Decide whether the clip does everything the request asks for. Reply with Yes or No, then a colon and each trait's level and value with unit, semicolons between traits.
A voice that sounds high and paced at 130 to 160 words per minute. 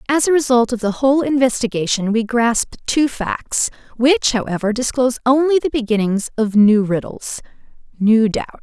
Yes: high, 240 Hz; average, 155 wpm